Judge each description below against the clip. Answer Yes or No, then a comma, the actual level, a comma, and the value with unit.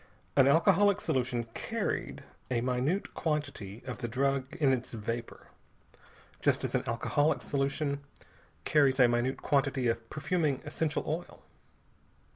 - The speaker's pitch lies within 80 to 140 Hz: Yes, low, 135 Hz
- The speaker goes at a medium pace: No, slow, 125 wpm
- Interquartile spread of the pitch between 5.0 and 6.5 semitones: No, average, 3.6 semitones